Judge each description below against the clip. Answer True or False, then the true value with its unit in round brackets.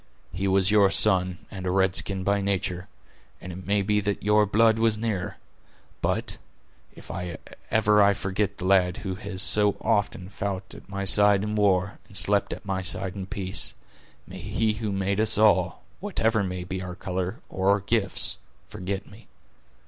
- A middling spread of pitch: False (1.9 semitones)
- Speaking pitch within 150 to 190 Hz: False (100 Hz)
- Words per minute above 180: False (175 wpm)